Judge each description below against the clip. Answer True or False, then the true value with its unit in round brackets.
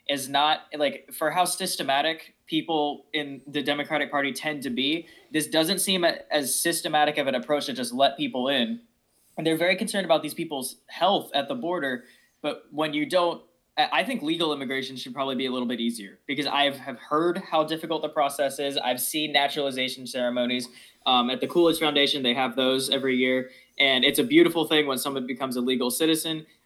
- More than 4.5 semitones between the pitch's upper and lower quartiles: False (3.3 semitones)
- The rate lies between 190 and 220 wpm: True (195 wpm)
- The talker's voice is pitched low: False (145 Hz)